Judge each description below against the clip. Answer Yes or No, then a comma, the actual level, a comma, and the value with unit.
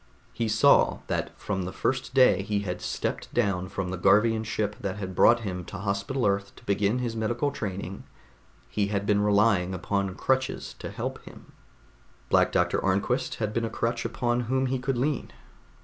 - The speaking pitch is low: Yes, low, 105 Hz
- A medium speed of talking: Yes, average, 180 wpm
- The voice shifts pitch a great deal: No, average, 3.3 semitones